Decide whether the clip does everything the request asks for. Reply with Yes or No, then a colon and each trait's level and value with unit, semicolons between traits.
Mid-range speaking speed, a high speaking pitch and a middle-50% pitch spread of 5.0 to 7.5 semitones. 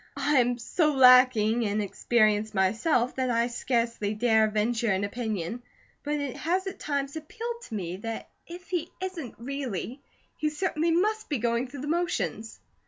Yes: average, 165 wpm; very high, 250 Hz; wide, 5.6 semitones